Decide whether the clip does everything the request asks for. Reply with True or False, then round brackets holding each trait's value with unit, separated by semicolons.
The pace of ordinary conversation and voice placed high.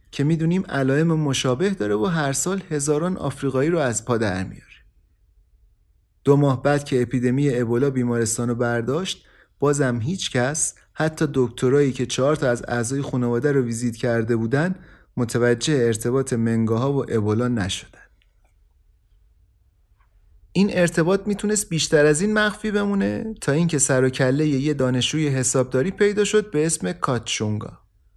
False (140 wpm; 130 Hz)